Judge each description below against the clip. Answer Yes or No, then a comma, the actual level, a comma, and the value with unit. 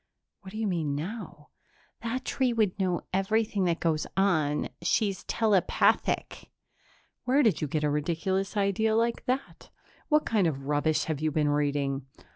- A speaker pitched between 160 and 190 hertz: Yes, medium, 185 Hz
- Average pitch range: No, wide, 6.4 semitones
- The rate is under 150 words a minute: No, average, 155 wpm